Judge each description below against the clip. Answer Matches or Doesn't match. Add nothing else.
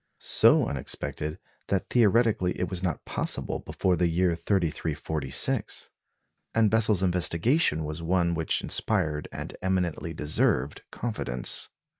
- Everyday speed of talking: Doesn't match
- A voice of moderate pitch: Doesn't match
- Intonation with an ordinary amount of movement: Matches